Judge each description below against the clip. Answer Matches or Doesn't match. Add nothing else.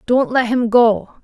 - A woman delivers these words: Matches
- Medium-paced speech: Matches